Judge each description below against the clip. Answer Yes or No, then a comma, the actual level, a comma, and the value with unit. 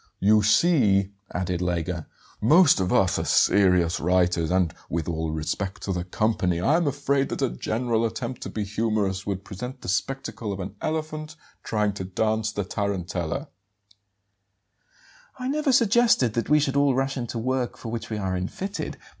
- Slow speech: No, average, 170 wpm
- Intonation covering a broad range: Yes, wide, 6.5 semitones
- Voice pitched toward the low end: Yes, low, 105 Hz